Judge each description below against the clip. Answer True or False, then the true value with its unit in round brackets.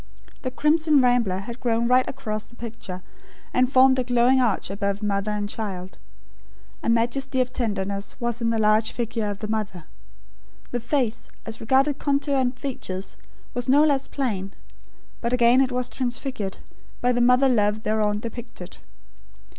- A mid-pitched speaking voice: False (235 Hz)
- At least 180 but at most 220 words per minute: False (160 wpm)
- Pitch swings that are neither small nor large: True (3.4 semitones)